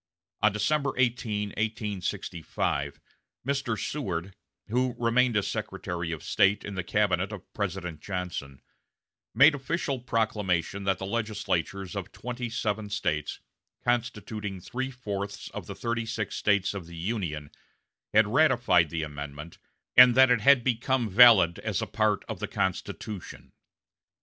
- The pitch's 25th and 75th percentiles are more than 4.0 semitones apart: Yes, average, 4.9 semitones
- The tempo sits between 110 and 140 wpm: Yes, slow, 135 wpm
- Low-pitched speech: Yes, low, 105 Hz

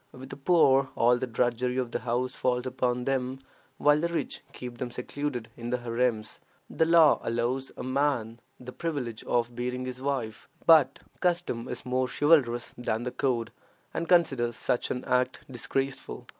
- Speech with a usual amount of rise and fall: No, narrow, 2.2 semitones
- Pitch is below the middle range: Yes, low, 125 Hz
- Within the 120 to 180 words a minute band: Yes, average, 170 wpm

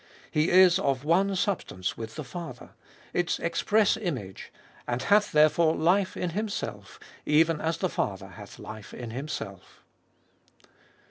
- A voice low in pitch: No, medium, 165 Hz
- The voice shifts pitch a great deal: Yes, wide, 5.9 semitones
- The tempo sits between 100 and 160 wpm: Yes, average, 140 wpm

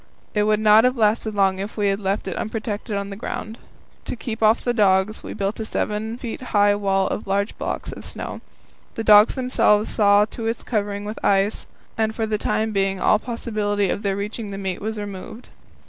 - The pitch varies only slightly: Yes, narrow, 1.6 semitones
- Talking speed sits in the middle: No, fast, 210 wpm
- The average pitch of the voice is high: Yes, high, 210 Hz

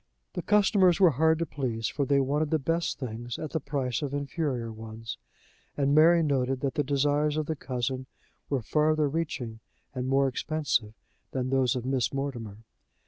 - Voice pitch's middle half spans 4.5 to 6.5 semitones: No, average, 3.4 semitones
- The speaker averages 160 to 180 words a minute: Yes, average, 175 wpm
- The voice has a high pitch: No, medium, 140 Hz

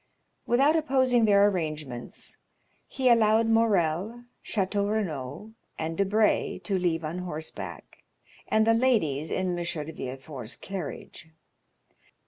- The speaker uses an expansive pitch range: Yes, wide, 5.9 semitones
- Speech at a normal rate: No, slow, 110 wpm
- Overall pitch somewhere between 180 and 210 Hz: Yes, high, 190 Hz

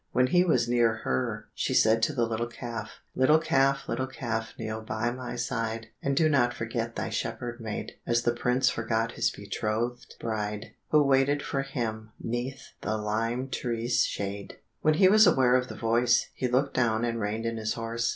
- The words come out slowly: No, average, 190 wpm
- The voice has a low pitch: Yes, low, 120 Hz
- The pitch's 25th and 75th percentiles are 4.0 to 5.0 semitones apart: No, narrow, 2.4 semitones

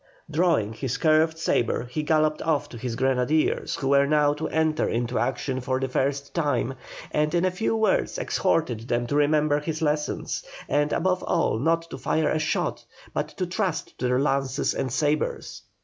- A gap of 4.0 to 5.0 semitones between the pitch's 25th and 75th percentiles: No, average, 3.3 semitones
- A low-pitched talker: No, medium, 150 Hz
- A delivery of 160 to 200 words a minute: Yes, average, 180 wpm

